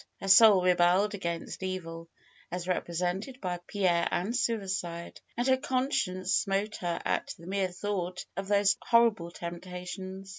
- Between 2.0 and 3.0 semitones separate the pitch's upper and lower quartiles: Yes, narrow, 2.5 semitones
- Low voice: No, medium, 185 Hz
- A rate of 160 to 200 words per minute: No, average, 140 wpm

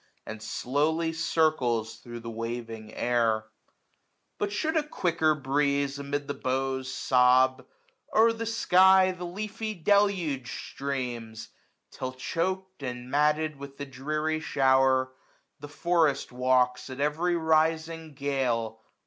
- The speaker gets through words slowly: Yes, slow, 125 wpm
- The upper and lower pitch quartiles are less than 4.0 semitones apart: No, average, 4.4 semitones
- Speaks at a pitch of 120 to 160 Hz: Yes, medium, 140 Hz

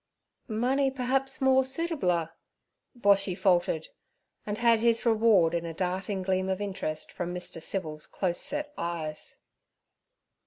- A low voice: No, high, 195 Hz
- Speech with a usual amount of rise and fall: No, wide, 6.0 semitones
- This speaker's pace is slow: Yes, slow, 125 wpm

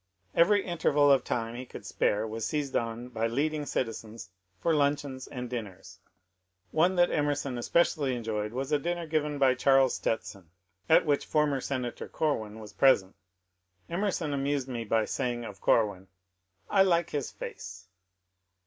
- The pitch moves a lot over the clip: No, average, 4.8 semitones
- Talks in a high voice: No, low, 130 Hz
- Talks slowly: No, average, 160 wpm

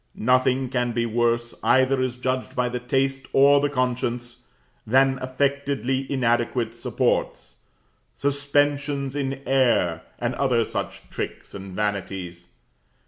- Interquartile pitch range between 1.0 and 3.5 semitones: Yes, narrow, 2.4 semitones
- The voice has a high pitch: No, low, 130 Hz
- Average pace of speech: No, slow, 120 wpm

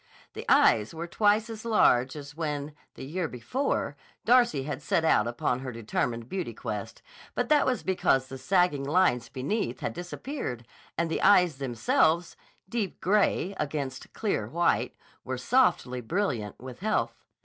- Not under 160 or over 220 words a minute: No, average, 150 wpm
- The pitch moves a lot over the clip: Yes, wide, 7.1 semitones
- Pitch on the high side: No, medium, 155 Hz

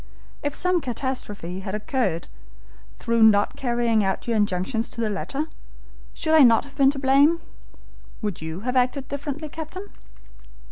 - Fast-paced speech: No, average, 150 wpm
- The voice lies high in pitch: Yes, high, 245 Hz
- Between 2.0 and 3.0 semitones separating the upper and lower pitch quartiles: No, average, 5.3 semitones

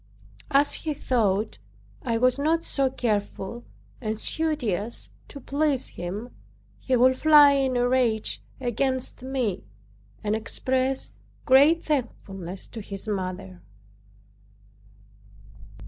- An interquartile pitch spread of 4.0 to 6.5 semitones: Yes, average, 4.5 semitones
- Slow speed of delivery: Yes, slow, 105 wpm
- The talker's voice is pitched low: No, very high, 250 Hz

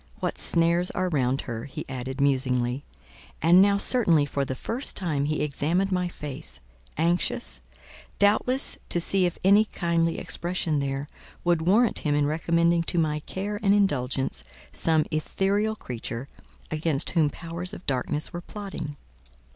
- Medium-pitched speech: Yes, medium, 165 Hz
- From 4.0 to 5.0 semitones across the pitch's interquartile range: Yes, average, 4.6 semitones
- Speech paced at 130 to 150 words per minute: Yes, average, 145 wpm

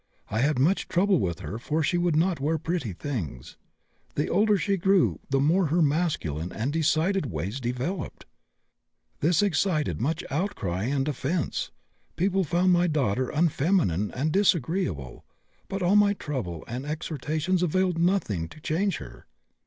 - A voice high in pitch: No, medium, 155 Hz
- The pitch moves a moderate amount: No, wide, 6.0 semitones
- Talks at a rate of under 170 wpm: Yes, average, 150 wpm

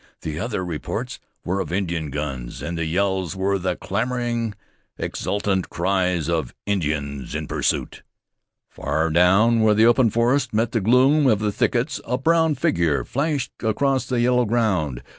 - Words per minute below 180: Yes, average, 155 wpm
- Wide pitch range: Yes, wide, 5.8 semitones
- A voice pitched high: No, low, 100 Hz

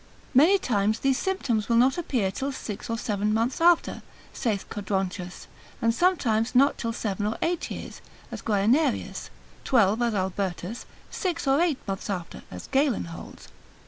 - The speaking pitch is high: Yes, high, 230 Hz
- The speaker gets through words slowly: No, average, 155 wpm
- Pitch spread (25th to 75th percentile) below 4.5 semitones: No, average, 5.3 semitones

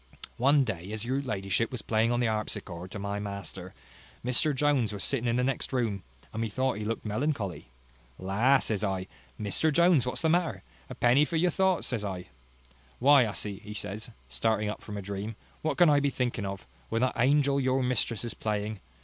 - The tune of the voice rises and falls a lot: No, average, 4.8 semitones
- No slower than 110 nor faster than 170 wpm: No, average, 200 wpm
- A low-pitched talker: Yes, low, 115 Hz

